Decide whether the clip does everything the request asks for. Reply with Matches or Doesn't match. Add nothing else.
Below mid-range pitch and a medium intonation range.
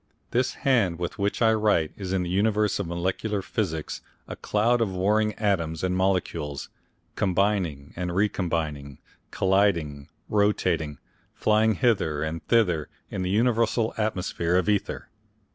Matches